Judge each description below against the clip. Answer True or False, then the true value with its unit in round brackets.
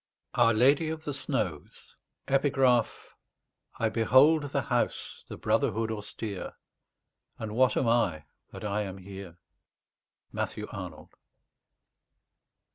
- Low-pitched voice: True (115 Hz)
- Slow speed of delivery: True (105 wpm)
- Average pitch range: True (4.5 semitones)